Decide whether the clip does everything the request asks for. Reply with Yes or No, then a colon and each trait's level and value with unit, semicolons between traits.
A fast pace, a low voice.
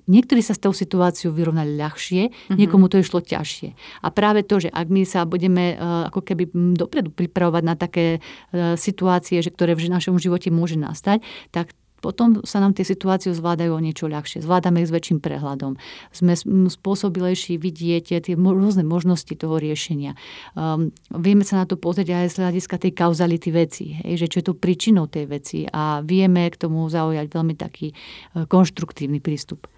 No: fast, 170 wpm; medium, 175 Hz